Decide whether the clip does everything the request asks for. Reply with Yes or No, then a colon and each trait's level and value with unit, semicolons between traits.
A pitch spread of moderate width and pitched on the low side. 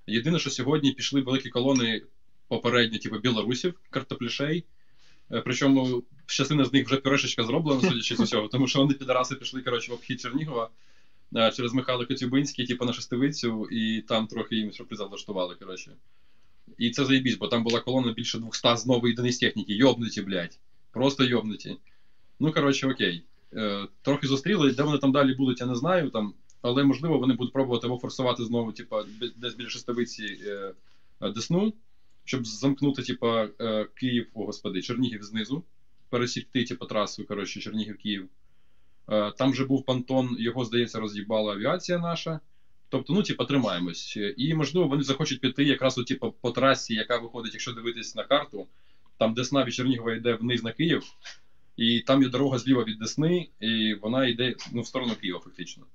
Yes: average, 3.0 semitones; low, 125 Hz